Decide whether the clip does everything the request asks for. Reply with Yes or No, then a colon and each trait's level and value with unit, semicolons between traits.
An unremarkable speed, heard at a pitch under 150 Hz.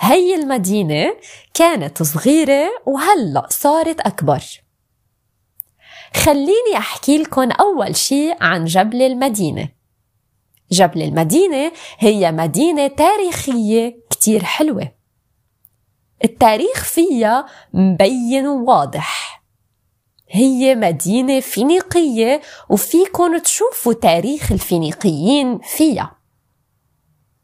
No: average, 75 wpm; very high, 250 Hz